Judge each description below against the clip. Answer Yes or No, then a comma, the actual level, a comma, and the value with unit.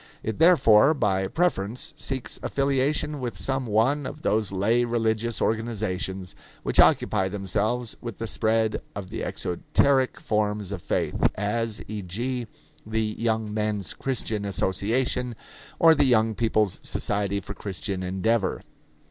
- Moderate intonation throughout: Yes, average, 3.4 semitones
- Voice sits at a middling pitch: No, low, 110 Hz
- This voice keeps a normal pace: No, slow, 130 wpm